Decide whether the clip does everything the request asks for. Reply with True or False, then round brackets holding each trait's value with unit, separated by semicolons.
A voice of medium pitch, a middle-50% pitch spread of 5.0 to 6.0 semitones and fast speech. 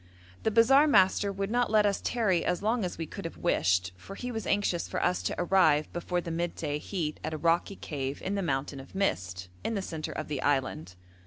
True (175 Hz; 5.3 semitones; 225 wpm)